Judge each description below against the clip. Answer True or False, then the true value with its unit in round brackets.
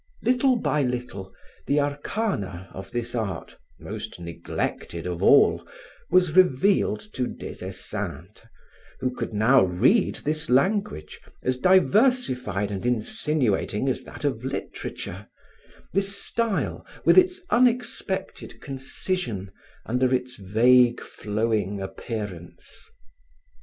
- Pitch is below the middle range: True (125 Hz)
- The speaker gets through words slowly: True (105 wpm)